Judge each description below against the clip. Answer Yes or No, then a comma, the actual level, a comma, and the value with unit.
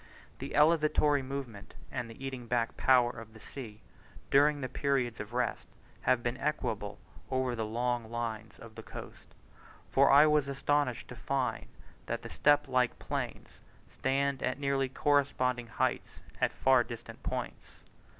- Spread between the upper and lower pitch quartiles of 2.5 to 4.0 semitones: Yes, average, 2.9 semitones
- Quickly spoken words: No, average, 145 wpm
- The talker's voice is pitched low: Yes, low, 130 Hz